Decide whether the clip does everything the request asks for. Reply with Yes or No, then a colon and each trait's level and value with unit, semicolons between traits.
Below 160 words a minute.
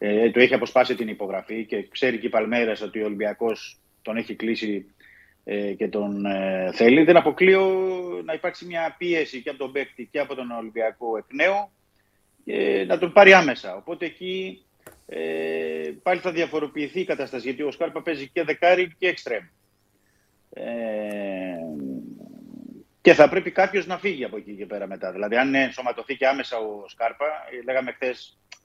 No: average, 165 wpm